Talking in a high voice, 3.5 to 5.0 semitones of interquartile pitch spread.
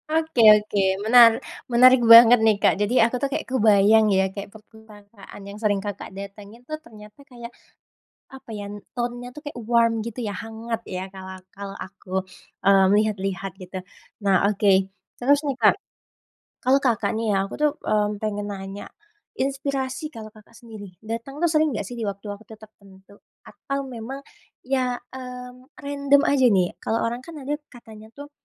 Yes: high, 225 Hz; average, 3.9 semitones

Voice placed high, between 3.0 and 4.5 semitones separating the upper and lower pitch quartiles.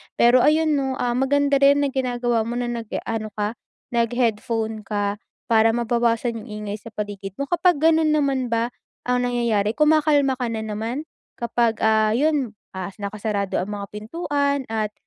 Yes: high, 235 Hz; average, 3.9 semitones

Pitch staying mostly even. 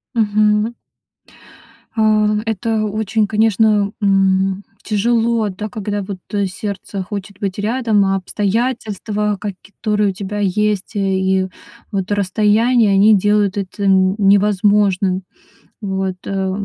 Yes: narrow, 1.8 semitones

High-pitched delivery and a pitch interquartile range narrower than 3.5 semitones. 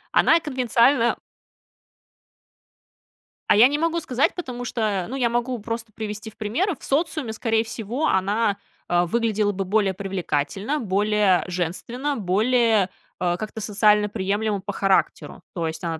No: high, 220 Hz; average, 3.8 semitones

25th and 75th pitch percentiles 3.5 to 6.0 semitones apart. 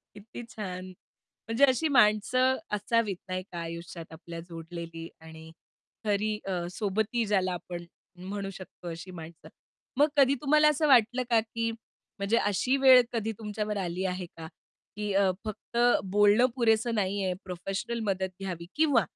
Yes: average, 4.2 semitones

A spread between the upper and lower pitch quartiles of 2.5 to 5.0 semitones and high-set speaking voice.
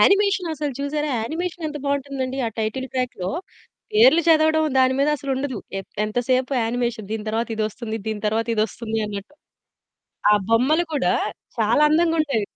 No: wide, 5.5 semitones; very high, 260 Hz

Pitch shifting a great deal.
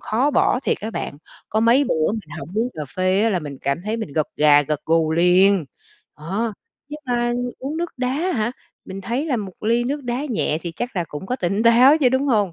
Yes: wide, 6.2 semitones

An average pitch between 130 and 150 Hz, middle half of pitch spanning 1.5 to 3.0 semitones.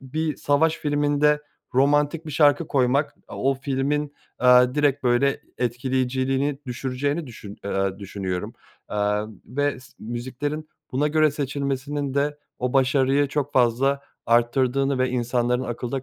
Yes: low, 135 Hz; average, 2.7 semitones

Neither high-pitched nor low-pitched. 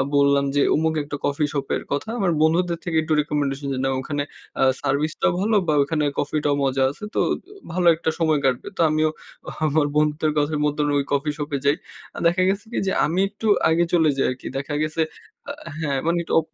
Yes: medium, 150 Hz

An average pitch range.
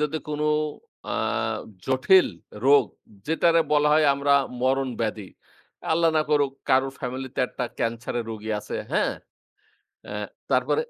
Yes: average, 3.1 semitones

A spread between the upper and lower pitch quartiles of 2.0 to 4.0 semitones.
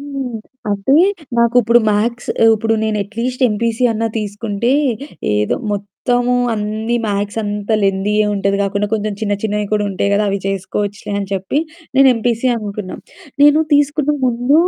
Yes: average, 2.9 semitones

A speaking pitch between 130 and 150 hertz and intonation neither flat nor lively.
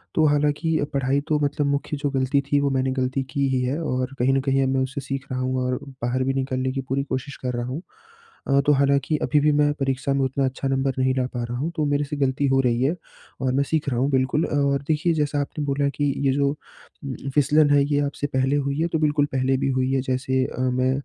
No: low, 135 Hz; narrow, 1.7 semitones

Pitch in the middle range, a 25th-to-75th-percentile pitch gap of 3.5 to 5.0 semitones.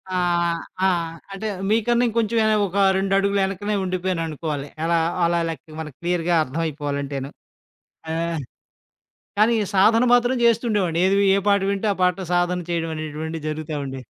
Yes: medium, 175 Hz; average, 3.8 semitones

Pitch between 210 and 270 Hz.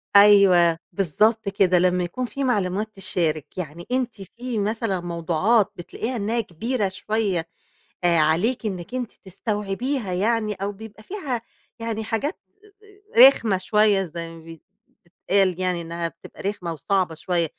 No: high, 200 Hz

